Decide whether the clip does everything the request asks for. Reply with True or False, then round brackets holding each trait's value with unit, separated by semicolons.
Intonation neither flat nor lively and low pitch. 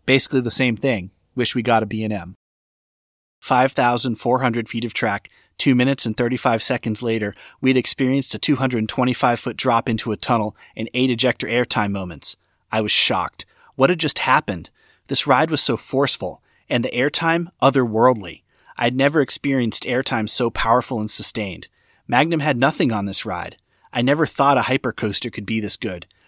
True (3.2 semitones; 120 Hz)